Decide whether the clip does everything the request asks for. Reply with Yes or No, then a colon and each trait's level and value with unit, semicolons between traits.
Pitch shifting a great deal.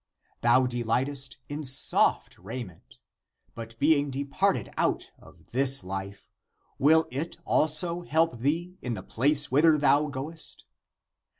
No: average, 4.1 semitones